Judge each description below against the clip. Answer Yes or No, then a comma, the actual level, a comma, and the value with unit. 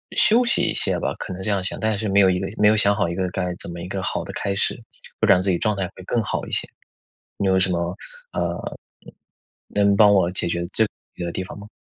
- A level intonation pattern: Yes, narrow, 2.2 semitones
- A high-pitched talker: No, very low, 95 Hz